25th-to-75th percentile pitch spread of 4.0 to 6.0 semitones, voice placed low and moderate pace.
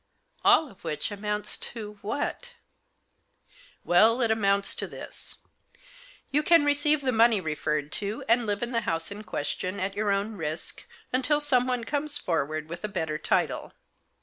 No: wide, 5.6 semitones; high, 210 Hz; average, 170 wpm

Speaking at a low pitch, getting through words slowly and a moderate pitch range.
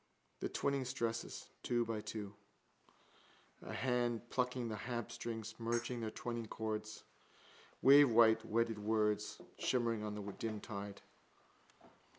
No: low, 115 Hz; slow, 115 wpm; narrow, 1.8 semitones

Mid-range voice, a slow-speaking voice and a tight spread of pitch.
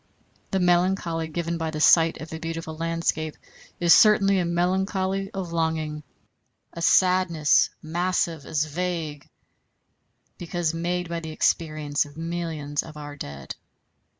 Yes: medium, 165 Hz; slow, 130 wpm; narrow, 2.2 semitones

